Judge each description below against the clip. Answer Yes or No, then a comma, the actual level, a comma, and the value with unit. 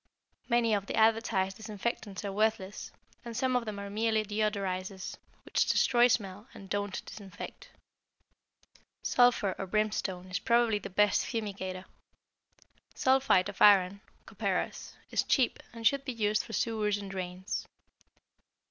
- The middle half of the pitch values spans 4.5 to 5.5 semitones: No, average, 2.8 semitones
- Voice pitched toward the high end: Yes, high, 210 Hz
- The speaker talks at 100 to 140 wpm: Yes, slow, 135 wpm